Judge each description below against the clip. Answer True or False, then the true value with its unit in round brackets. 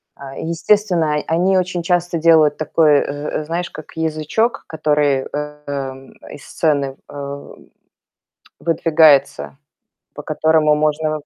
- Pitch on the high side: False (155 Hz)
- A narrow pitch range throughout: True (2.3 semitones)